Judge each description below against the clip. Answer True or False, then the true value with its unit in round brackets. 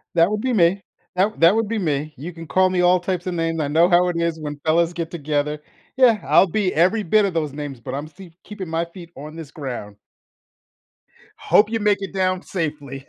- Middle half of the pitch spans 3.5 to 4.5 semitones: True (3.8 semitones)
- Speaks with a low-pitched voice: False (170 Hz)